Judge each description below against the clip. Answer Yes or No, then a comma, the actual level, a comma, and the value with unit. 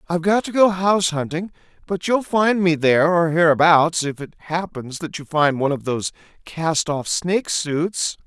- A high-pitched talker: No, medium, 165 Hz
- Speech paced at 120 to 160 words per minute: No, average, 190 wpm